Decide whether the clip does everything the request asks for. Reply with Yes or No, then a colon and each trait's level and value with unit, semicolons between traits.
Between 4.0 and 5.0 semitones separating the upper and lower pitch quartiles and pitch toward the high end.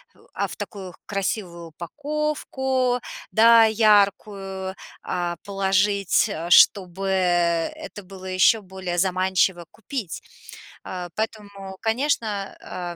No: average, 3.2 semitones; high, 195 Hz